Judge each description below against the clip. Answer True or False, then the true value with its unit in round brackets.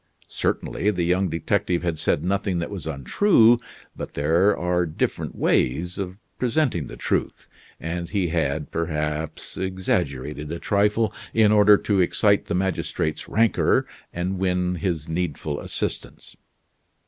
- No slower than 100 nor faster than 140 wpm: True (135 wpm)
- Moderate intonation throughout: True (3.7 semitones)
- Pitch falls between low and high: False (90 Hz)